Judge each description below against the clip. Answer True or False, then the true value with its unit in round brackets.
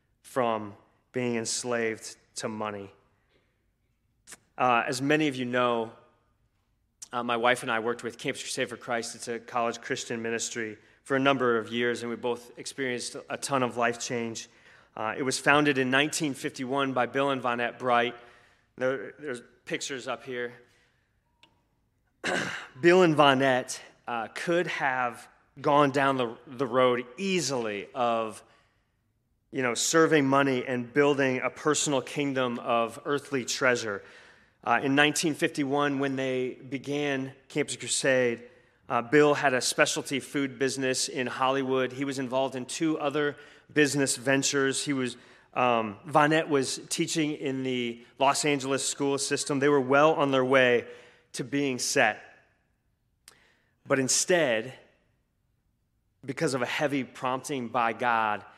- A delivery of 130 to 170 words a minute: True (140 wpm)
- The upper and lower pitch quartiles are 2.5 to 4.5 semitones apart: True (2.9 semitones)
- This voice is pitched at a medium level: False (130 Hz)